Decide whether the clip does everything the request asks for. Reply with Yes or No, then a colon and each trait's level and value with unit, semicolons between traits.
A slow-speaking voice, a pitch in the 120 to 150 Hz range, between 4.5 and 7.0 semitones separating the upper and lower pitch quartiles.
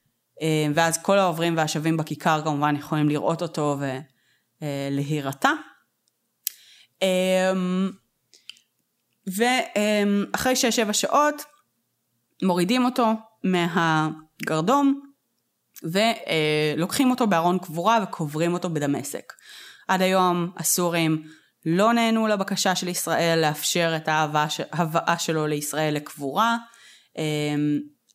No: slow, 80 wpm; medium, 170 Hz; average, 5.1 semitones